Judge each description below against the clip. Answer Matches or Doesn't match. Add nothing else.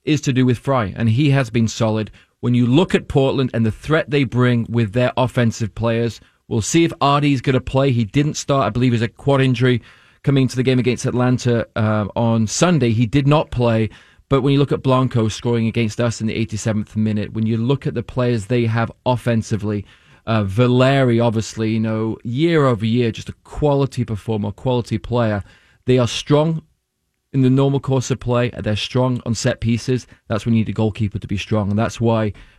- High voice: Doesn't match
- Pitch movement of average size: Matches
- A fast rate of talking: Matches